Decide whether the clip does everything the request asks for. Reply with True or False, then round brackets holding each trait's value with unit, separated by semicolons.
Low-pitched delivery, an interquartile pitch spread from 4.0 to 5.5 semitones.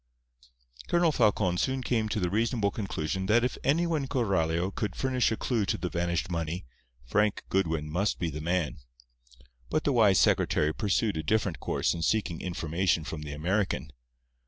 True (95 Hz; 5.2 semitones)